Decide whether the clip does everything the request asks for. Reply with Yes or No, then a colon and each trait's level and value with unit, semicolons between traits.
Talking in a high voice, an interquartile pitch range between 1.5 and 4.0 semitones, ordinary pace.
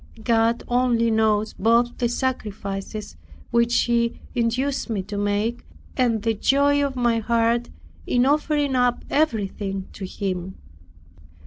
No: high, 230 Hz; average, 2.7 semitones; slow, 125 wpm